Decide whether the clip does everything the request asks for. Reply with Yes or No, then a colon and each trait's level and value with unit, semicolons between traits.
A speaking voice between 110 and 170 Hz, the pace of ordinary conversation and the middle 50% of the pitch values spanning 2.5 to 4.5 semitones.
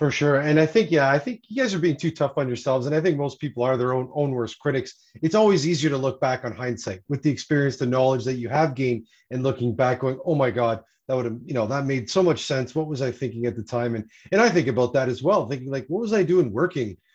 No: low, 135 Hz; fast, 290 wpm; average, 3.7 semitones